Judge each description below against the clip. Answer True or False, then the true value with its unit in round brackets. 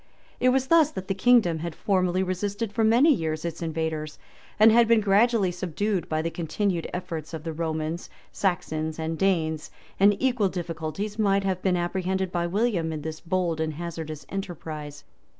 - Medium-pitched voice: True (180 Hz)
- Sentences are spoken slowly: False (170 wpm)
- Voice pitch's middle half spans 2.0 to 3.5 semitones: False (4.1 semitones)